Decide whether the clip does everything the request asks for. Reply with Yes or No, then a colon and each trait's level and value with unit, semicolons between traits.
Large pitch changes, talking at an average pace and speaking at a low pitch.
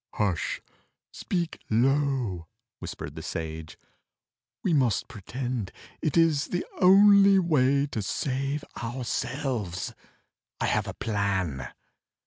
No: wide, 6.7 semitones; slow, 105 wpm; low, 130 Hz